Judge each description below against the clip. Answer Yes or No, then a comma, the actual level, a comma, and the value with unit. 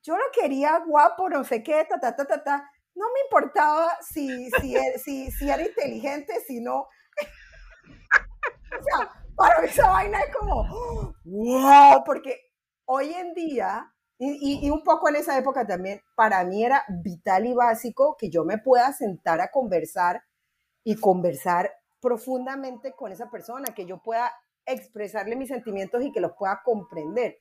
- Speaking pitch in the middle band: No, very high, 255 Hz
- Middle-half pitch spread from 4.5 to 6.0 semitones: Yes, average, 5.3 semitones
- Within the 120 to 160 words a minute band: No, average, 170 wpm